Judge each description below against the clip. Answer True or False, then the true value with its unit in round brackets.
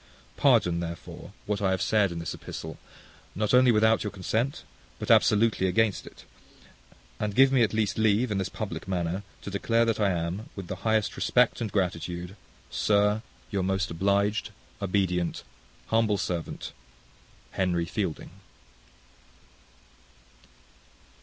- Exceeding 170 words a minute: False (135 wpm)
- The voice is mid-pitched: False (100 Hz)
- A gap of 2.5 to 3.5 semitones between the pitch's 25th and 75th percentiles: True (3.0 semitones)